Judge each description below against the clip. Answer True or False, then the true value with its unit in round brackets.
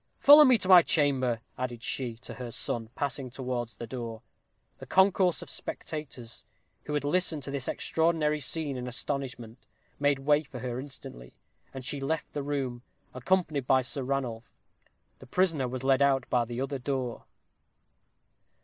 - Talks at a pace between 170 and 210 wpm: False (160 wpm)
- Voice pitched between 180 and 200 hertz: False (135 Hz)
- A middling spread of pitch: True (3.1 semitones)